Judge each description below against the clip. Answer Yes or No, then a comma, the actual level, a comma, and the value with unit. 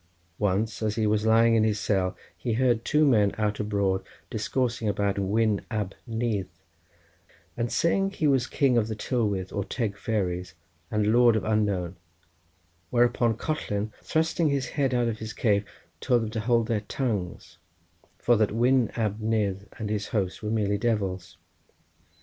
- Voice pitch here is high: No, low, 110 Hz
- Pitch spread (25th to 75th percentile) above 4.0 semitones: No, average, 2.7 semitones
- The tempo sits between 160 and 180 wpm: Yes, average, 165 wpm